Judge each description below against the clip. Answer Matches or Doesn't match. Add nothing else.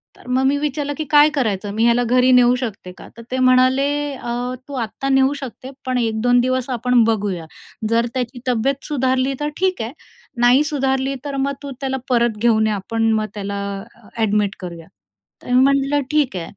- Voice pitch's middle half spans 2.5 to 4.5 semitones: Matches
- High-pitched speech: Matches